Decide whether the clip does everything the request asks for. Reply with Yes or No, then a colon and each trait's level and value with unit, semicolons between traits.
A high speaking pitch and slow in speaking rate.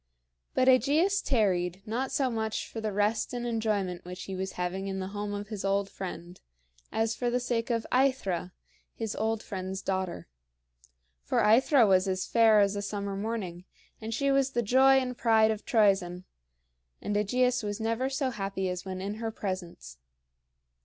No: high, 210 Hz; average, 175 wpm